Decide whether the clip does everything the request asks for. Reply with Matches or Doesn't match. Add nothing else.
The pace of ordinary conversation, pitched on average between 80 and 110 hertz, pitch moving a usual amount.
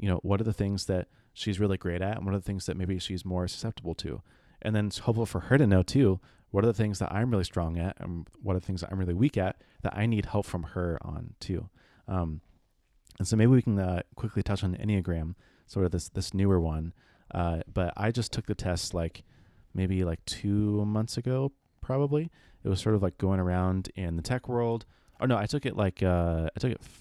Doesn't match